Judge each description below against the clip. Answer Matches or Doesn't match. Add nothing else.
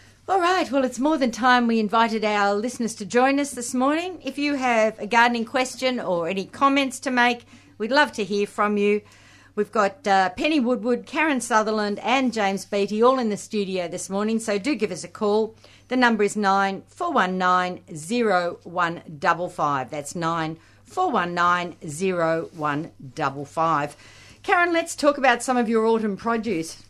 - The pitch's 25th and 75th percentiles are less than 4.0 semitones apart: Doesn't match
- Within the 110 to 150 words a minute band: Doesn't match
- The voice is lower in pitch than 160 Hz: Doesn't match